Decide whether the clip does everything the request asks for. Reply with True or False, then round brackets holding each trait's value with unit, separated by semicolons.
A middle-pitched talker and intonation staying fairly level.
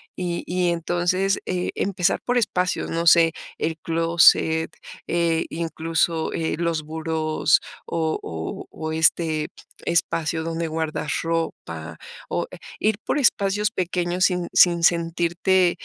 True (170 Hz; 1.8 semitones)